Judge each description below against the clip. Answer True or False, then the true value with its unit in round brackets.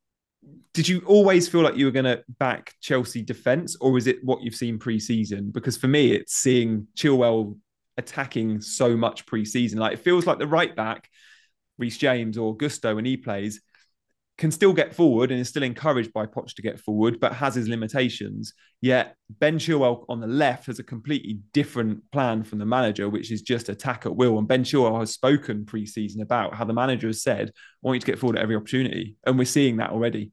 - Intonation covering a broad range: False (3.0 semitones)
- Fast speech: True (215 wpm)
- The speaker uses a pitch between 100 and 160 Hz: True (120 Hz)